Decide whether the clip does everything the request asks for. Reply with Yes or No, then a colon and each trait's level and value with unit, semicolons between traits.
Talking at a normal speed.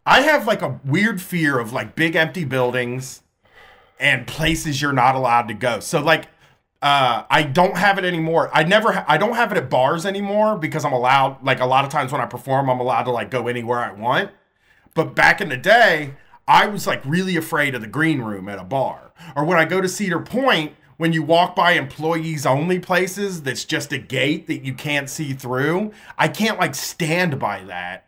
No: fast, 215 wpm